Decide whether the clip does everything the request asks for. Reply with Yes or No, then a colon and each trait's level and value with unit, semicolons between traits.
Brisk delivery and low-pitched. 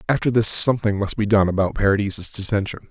No: average, 185 wpm; low, 105 Hz